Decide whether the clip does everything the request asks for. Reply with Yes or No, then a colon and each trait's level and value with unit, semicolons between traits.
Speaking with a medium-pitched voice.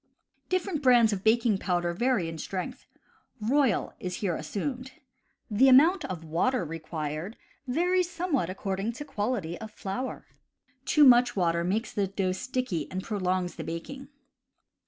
No: high, 210 Hz